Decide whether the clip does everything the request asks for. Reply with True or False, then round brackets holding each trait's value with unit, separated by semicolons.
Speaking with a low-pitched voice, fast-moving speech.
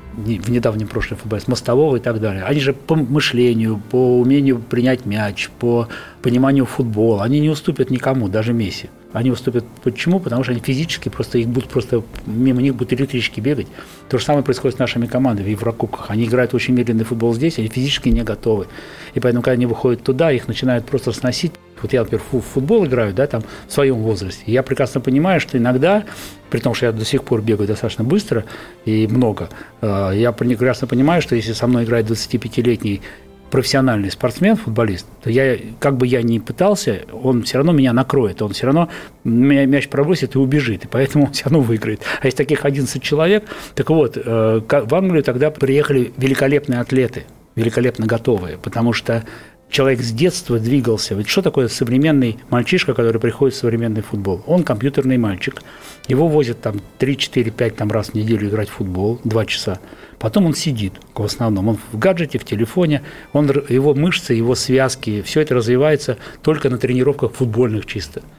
True (125 Hz; 180 wpm)